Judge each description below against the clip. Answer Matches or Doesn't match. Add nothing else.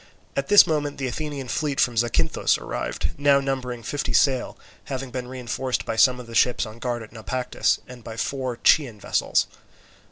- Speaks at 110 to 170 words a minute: Doesn't match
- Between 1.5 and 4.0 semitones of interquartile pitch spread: Matches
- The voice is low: Matches